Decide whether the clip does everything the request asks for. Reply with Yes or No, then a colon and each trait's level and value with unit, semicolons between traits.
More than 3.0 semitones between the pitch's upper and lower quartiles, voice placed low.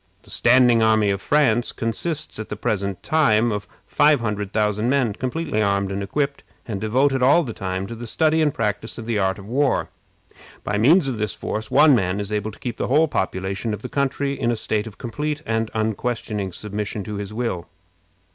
Yes: average, 4.4 semitones; low, 110 Hz